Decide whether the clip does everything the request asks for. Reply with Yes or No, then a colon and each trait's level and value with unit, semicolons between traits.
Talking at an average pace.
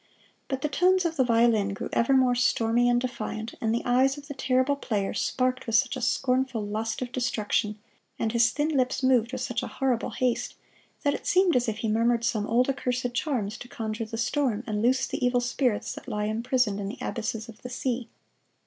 No: fast, 210 wpm